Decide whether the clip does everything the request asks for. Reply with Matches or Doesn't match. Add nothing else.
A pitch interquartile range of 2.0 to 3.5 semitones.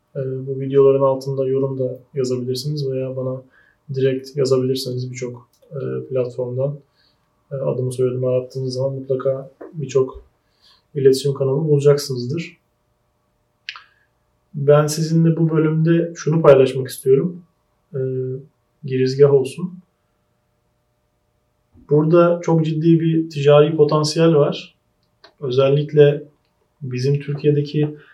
Matches